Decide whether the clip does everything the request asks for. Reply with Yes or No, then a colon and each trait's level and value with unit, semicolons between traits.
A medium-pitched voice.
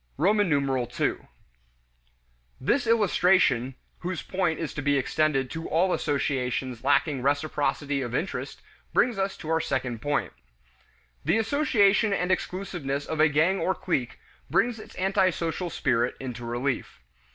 Yes: medium, 155 Hz